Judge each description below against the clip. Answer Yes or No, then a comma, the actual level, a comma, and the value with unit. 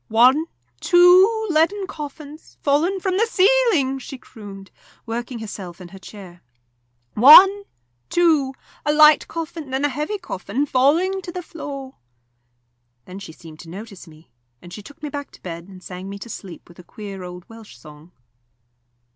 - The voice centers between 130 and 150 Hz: No, very high, 265 Hz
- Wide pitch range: Yes, wide, 9.0 semitones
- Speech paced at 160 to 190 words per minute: Yes, average, 165 wpm